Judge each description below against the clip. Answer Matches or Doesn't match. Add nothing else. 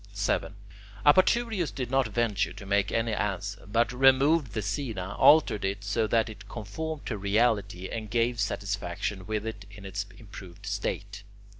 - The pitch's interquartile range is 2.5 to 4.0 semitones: Matches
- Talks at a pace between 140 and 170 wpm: Matches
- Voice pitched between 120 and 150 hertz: Doesn't match